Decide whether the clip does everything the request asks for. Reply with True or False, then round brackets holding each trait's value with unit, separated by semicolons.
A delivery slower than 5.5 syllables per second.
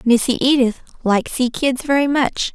True (4.5 syllables/s)